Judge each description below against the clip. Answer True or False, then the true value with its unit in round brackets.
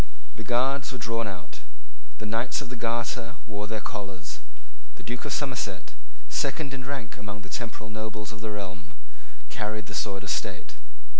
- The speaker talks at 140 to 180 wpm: True (170 wpm)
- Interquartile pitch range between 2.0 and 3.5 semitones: True (2.9 semitones)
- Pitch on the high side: False (110 Hz)